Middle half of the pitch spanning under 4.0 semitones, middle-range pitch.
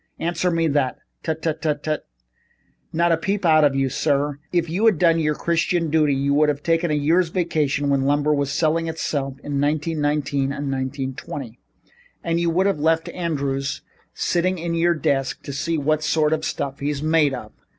Yes: average, 2.8 semitones; medium, 155 Hz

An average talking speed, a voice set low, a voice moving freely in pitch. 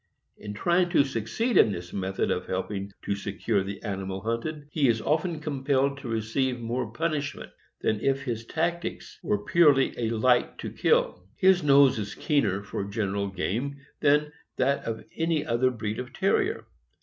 Yes: average, 165 wpm; low, 120 Hz; wide, 6.0 semitones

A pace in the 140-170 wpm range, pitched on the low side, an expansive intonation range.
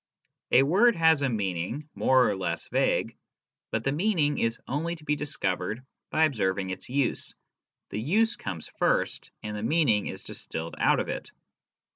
Yes: average, 165 wpm; low, 130 Hz; wide, 7.0 semitones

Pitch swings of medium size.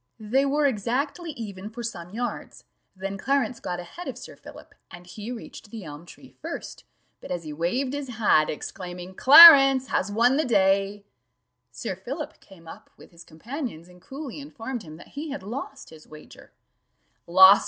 No: wide, 7.1 semitones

